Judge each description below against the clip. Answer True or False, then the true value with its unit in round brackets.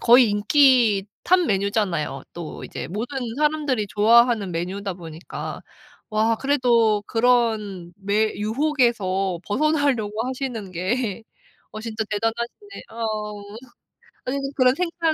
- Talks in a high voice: True (220 Hz)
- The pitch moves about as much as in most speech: True (3.9 semitones)